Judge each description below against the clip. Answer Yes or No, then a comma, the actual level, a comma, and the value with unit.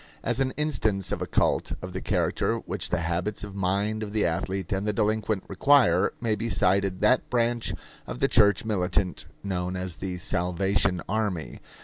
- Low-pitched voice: Yes, low, 100 Hz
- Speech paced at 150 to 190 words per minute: Yes, average, 175 wpm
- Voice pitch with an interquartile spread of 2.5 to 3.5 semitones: Yes, average, 3.0 semitones